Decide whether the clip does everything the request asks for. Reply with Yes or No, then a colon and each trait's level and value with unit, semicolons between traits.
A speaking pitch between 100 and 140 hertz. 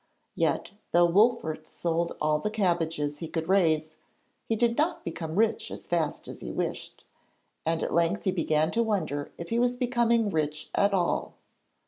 No: medium, 170 Hz